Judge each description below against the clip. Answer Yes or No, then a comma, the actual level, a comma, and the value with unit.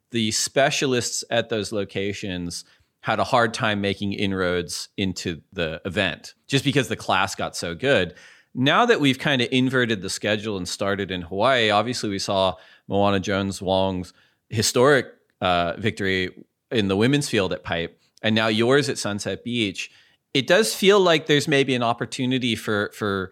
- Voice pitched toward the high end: No, low, 105 Hz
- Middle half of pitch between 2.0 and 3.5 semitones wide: No, average, 4.3 semitones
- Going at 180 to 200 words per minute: No, average, 165 wpm